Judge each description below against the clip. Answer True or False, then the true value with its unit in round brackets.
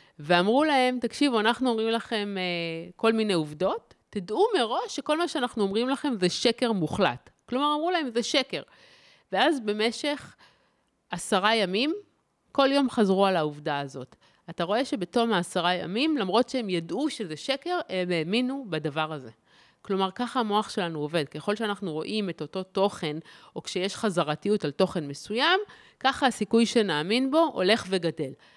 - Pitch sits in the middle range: False (210 Hz)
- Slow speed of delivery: False (150 wpm)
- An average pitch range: False (6.4 semitones)